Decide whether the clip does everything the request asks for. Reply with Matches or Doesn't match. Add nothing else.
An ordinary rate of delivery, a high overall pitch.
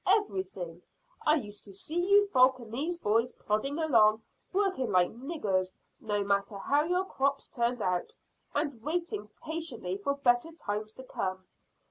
Matches